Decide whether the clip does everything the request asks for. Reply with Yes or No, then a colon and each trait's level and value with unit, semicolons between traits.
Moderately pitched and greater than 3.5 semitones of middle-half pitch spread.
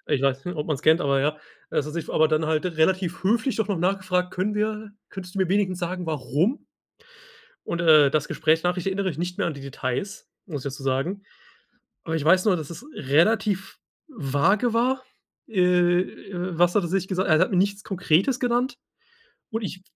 Yes: medium, 180 Hz; average, 4.1 semitones